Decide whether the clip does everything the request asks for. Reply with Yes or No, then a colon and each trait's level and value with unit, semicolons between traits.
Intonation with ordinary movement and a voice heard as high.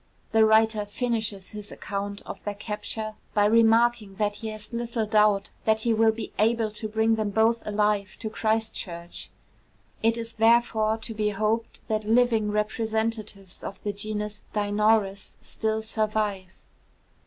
No: narrow, 1.3 semitones; high, 215 Hz